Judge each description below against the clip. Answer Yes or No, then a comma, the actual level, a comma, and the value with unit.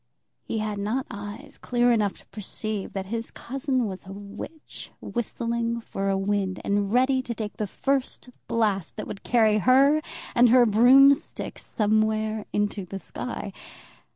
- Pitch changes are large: No, average, 3.1 semitones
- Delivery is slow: No, average, 155 wpm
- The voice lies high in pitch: Yes, high, 220 Hz